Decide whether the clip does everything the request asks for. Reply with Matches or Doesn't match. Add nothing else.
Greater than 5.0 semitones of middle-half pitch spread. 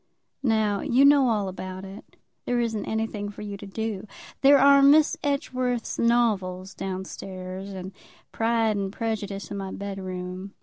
Doesn't match